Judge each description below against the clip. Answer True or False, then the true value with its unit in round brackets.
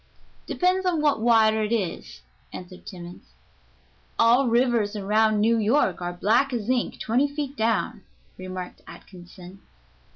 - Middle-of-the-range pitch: False (220 Hz)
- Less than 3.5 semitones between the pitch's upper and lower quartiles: False (4.3 semitones)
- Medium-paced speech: False (130 wpm)